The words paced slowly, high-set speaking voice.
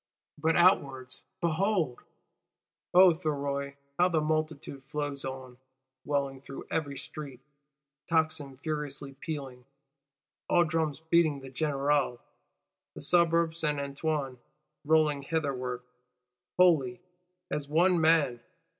No: slow, 100 wpm; medium, 150 Hz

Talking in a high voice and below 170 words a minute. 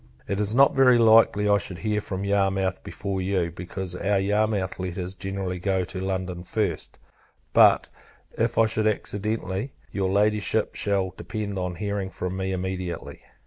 No: very low, 95 Hz; average, 155 wpm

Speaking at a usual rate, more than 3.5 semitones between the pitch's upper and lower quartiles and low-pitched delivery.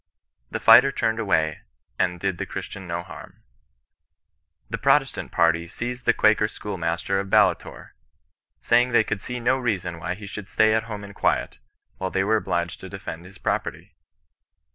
Yes: average, 165 wpm; average, 4.0 semitones; low, 100 Hz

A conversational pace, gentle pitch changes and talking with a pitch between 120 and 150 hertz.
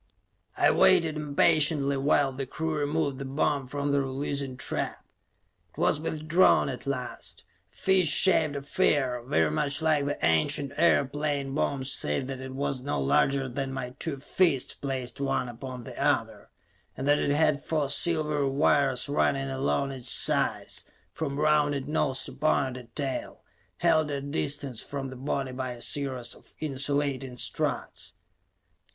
Yes: average, 155 wpm; narrow, 1.9 semitones; medium, 140 Hz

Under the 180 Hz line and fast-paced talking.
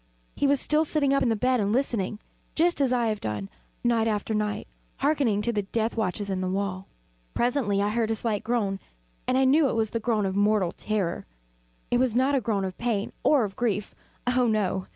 No: high, 220 Hz; fast, 215 wpm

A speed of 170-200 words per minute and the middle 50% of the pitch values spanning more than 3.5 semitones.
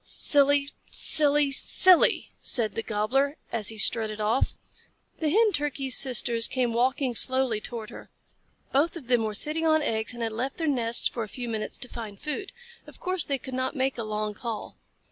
Yes: average, 185 wpm; average, 4.2 semitones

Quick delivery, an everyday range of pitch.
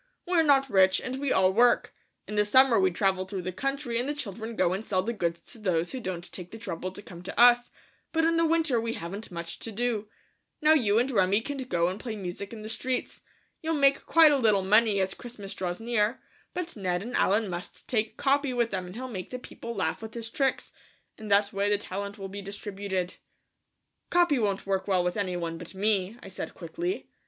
Yes: fast, 225 wpm; average, 4.6 semitones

